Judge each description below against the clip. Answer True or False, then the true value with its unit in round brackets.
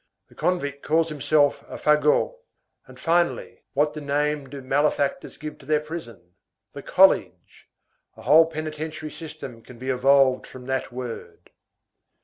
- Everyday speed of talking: False (130 wpm)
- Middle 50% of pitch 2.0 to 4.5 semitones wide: True (2.8 semitones)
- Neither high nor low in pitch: True (150 Hz)